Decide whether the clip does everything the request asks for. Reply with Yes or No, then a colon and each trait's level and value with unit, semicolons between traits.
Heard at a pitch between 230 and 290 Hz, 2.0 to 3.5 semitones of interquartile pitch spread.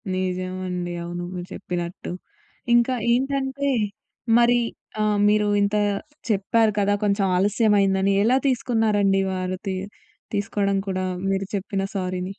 No: high, 200 Hz; average, 2.7 semitones